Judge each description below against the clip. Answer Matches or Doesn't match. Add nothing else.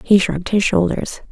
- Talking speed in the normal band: Matches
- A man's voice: Doesn't match